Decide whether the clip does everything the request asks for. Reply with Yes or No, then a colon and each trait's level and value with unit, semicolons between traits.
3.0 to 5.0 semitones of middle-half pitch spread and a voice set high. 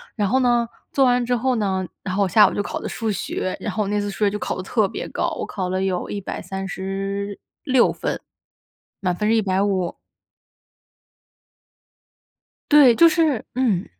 Yes: average, 3.7 semitones; high, 205 Hz